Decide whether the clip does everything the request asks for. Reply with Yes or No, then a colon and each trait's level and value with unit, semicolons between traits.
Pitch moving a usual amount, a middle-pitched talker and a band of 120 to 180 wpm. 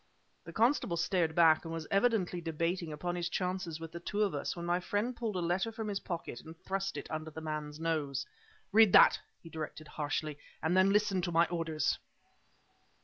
No: average, 3.3 semitones; medium, 170 Hz; average, 200 wpm